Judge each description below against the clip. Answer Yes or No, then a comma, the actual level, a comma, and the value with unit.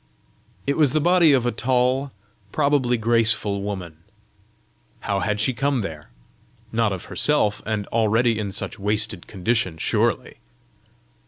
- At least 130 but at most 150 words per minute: Yes, slow, 135 wpm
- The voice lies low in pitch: Yes, low, 110 Hz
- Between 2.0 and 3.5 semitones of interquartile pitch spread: No, average, 4.1 semitones